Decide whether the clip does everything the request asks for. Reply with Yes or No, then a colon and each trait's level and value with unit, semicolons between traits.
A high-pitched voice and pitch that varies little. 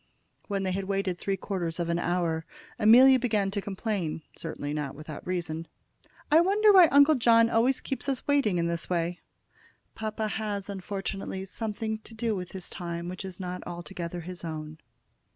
No: high, 195 Hz; average, 4.3 semitones